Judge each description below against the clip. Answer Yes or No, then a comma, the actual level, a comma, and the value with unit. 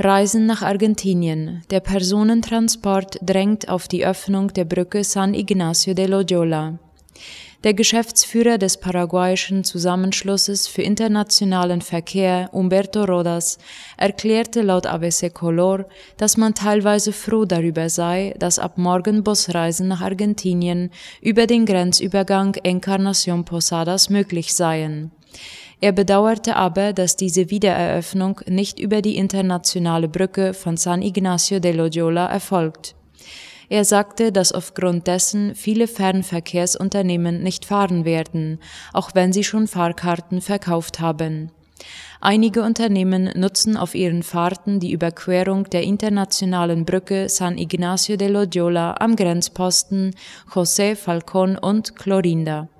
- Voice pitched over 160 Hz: Yes, high, 190 Hz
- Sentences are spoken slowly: Yes, slow, 115 wpm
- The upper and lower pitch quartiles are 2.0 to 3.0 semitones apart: Yes, narrow, 2.4 semitones